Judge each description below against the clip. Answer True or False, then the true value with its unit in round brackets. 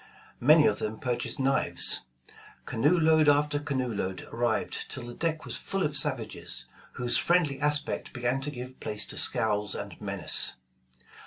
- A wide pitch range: False (3.6 semitones)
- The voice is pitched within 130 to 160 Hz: True (135 Hz)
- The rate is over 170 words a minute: False (155 wpm)